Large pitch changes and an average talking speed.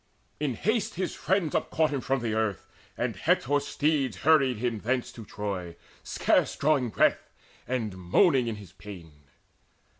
Yes: wide, 5.9 semitones; average, 150 wpm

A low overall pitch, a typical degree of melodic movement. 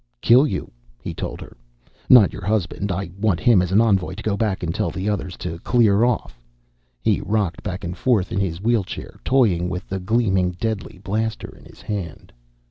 Yes: low, 100 Hz; average, 3.5 semitones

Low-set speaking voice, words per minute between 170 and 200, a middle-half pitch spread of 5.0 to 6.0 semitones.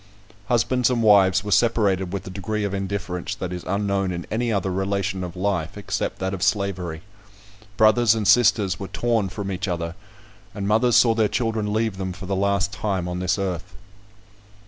No: low, 100 Hz; average, 185 wpm; narrow, 2.5 semitones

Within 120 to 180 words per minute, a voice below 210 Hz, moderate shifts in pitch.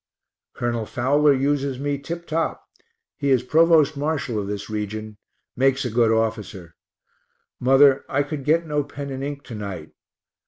Yes: average, 155 wpm; low, 135 Hz; average, 4.4 semitones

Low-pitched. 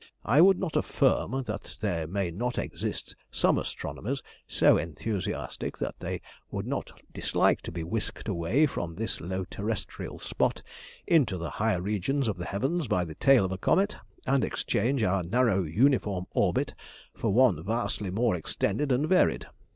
Yes: low, 105 Hz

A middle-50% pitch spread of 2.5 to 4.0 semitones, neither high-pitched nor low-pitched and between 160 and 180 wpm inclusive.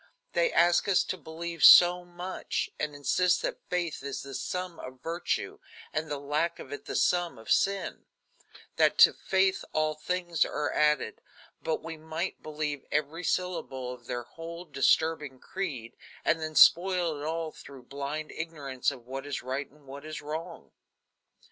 Yes: average, 3.5 semitones; medium, 155 Hz; average, 165 wpm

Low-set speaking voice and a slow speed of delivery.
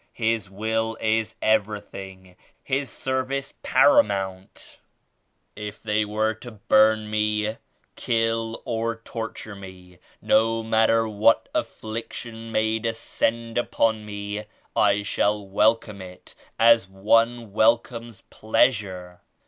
Yes: low, 110 Hz; slow, 110 wpm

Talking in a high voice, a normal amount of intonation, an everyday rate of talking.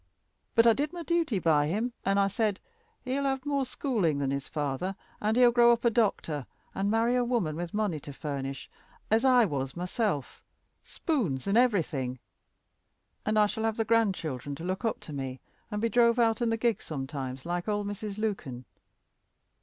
No: high, 205 Hz; wide, 7.7 semitones; average, 185 wpm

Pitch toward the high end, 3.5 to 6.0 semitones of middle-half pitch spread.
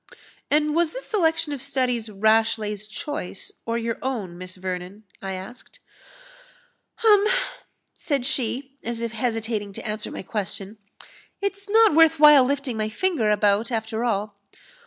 Yes: high, 230 Hz; wide, 5.6 semitones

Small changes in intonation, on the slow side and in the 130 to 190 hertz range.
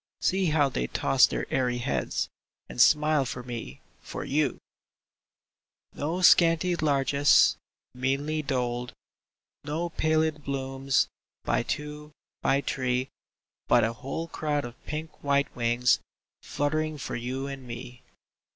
No: average, 3.5 semitones; slow, 125 wpm; medium, 140 Hz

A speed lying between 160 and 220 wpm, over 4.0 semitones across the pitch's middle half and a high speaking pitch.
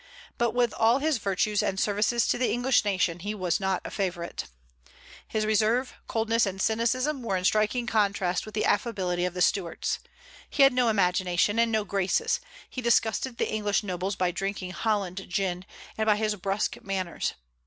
No: average, 175 wpm; average, 3.4 semitones; high, 210 Hz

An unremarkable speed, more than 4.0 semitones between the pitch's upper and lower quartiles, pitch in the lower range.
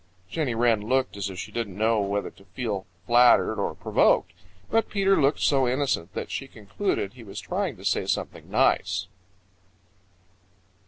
Yes: average, 160 wpm; average, 5.2 semitones; low, 120 Hz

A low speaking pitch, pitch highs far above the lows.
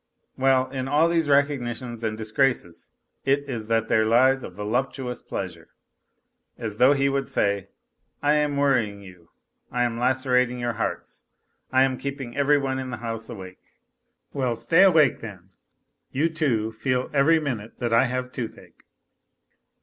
No: low, 125 Hz; average, 3.5 semitones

